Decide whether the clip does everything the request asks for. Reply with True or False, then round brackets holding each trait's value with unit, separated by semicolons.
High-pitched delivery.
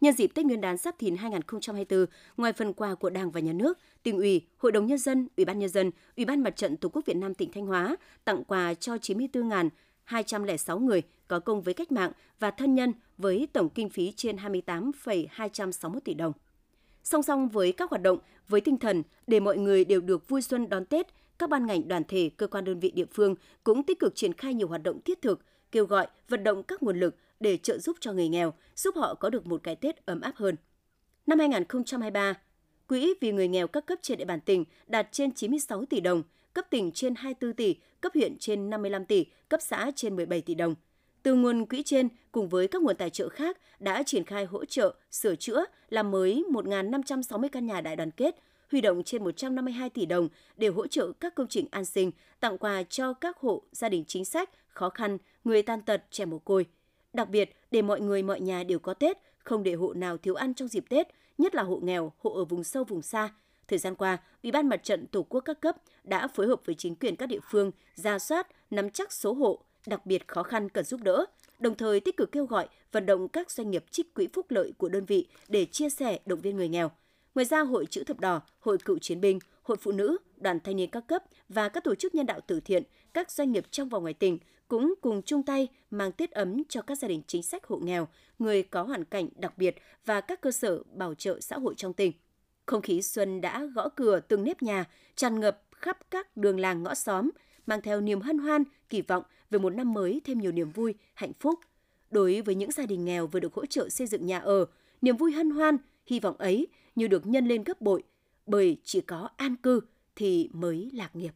True (220 Hz)